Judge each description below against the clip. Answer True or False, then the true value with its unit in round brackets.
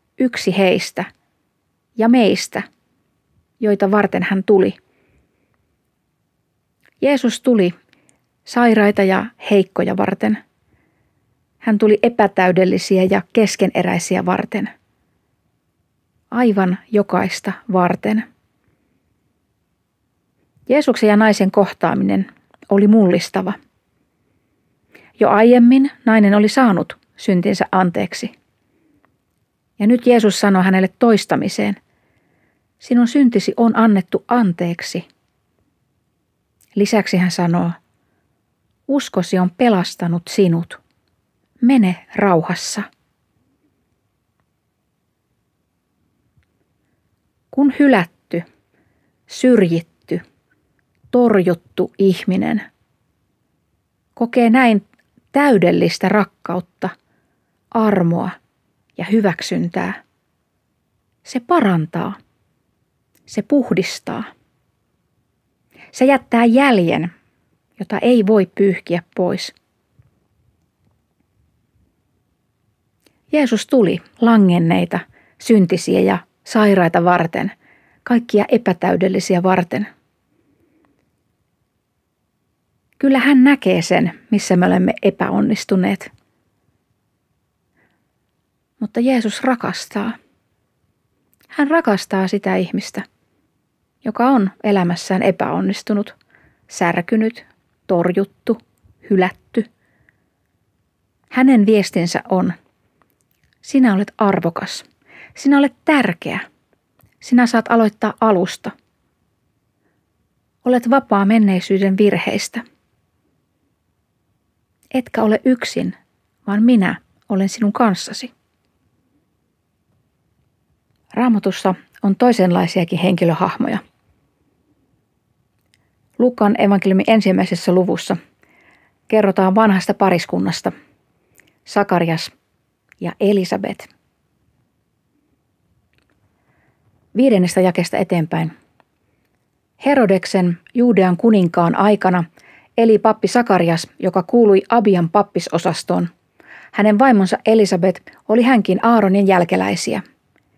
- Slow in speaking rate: True (70 wpm)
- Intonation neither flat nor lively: True (4.0 semitones)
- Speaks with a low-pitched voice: False (205 Hz)